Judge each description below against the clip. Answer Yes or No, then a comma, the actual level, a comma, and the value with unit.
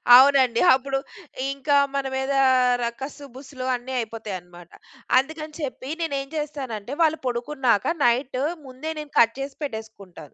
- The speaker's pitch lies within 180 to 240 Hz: No, very high, 265 Hz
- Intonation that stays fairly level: No, average, 3.2 semitones